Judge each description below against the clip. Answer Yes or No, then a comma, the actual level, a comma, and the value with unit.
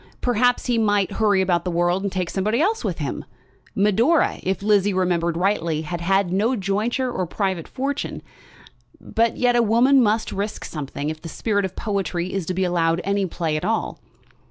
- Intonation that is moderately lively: Yes, average, 4.2 semitones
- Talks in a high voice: Yes, high, 195 Hz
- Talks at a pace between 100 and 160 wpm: No, average, 185 wpm